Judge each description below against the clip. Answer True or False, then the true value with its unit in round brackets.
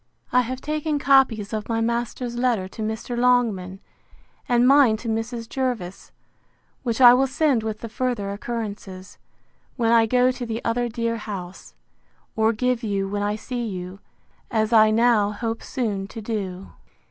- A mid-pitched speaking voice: False (230 Hz)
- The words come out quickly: False (160 wpm)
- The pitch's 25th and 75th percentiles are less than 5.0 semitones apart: True (2.7 semitones)